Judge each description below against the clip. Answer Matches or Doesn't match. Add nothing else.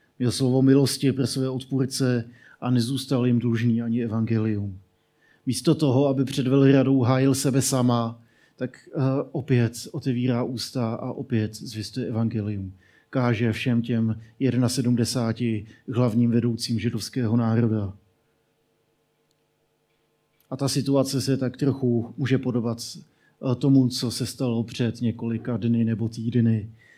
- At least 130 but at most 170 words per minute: Doesn't match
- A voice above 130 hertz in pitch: Doesn't match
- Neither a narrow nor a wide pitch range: Doesn't match